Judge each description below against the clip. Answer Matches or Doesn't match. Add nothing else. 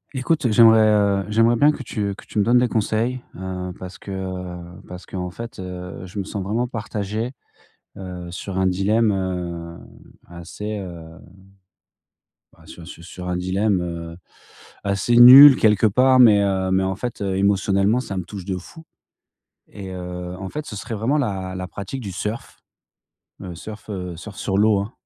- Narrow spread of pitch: Doesn't match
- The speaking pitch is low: Matches